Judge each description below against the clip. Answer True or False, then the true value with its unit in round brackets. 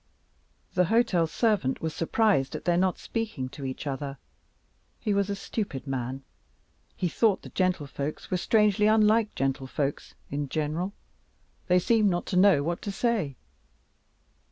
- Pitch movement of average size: False (6.6 semitones)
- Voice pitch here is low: False (180 Hz)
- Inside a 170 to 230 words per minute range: False (145 wpm)